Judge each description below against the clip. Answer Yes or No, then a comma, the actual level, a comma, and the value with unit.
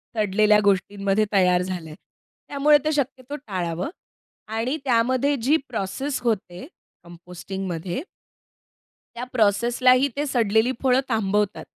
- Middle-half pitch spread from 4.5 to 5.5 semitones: Yes, average, 5.1 semitones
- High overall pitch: Yes, high, 215 Hz